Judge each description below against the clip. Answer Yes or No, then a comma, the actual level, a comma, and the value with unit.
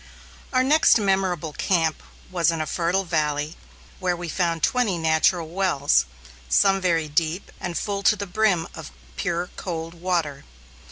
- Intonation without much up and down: No, average, 3.1 semitones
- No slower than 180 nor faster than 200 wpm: No, average, 150 wpm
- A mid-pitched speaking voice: Yes, medium, 175 Hz